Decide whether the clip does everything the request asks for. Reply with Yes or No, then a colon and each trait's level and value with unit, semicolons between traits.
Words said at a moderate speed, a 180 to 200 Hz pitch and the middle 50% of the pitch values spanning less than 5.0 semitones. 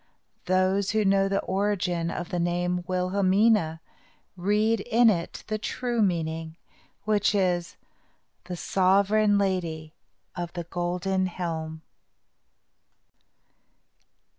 No: slow, 100 wpm; medium, 185 Hz; narrow, 2.6 semitones